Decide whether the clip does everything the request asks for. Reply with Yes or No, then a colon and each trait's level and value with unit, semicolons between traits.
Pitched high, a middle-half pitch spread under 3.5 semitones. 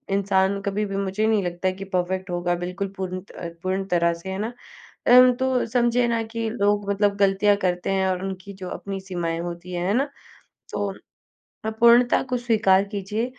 Yes: high, 195 Hz; average, 2.9 semitones